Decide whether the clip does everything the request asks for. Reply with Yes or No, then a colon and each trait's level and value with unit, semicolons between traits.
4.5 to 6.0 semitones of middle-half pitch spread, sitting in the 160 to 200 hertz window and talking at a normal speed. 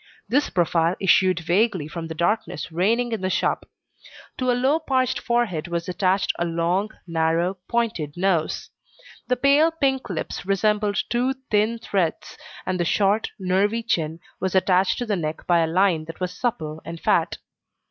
Yes: average, 5.2 semitones; high, 190 Hz; average, 165 wpm